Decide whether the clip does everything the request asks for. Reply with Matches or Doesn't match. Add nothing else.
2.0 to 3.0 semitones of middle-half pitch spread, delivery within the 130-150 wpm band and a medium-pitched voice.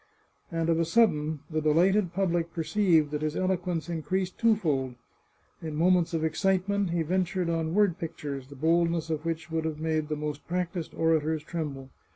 Doesn't match